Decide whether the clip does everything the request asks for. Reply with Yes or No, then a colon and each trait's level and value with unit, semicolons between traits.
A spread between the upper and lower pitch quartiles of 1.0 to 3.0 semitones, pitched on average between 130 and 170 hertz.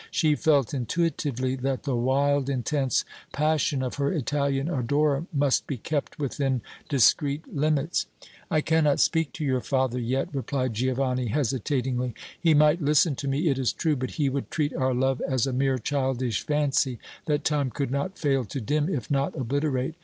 Yes: narrow, 2.4 semitones; medium, 140 Hz